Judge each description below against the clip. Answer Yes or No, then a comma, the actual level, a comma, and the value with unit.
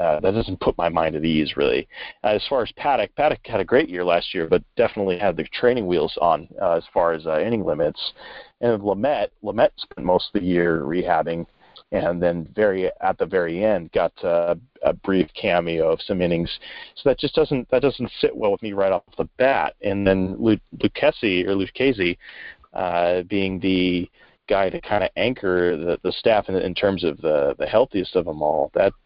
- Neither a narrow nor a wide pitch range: Yes, average, 4.5 semitones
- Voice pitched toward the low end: Yes, very low, 95 Hz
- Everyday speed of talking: No, fast, 210 wpm